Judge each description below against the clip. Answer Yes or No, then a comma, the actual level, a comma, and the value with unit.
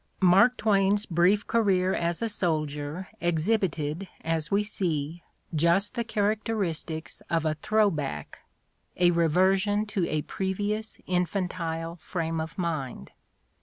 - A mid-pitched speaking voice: Yes, medium, 180 Hz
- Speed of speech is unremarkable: No, slow, 125 wpm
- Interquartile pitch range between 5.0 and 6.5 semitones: No, average, 4.1 semitones